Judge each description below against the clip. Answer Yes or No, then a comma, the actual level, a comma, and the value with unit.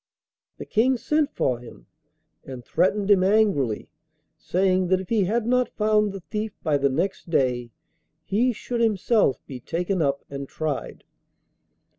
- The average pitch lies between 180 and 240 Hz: Yes, high, 190 Hz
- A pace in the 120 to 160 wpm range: Yes, average, 150 wpm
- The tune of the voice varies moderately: No, wide, 7.4 semitones